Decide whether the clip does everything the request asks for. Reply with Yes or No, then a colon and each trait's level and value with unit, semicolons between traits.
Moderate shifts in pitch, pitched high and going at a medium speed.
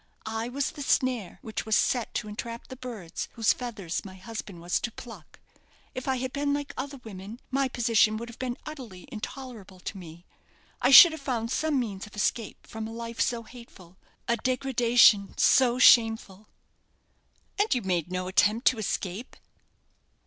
Yes: average, 3.7 semitones; high, 230 Hz; average, 170 wpm